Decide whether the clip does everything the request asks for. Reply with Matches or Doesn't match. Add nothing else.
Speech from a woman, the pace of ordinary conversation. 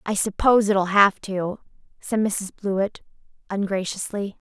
Doesn't match